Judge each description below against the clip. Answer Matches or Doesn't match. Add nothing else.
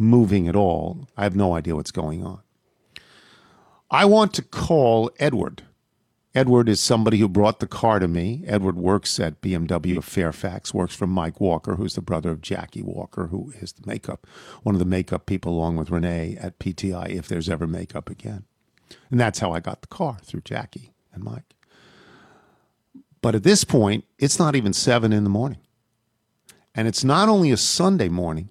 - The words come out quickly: Doesn't match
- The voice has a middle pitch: Doesn't match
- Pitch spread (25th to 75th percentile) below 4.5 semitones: Doesn't match